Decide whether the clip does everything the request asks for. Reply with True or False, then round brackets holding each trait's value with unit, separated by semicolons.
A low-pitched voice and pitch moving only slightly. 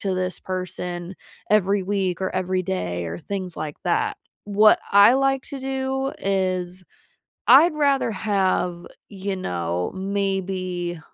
False (190 Hz; 2.2 semitones)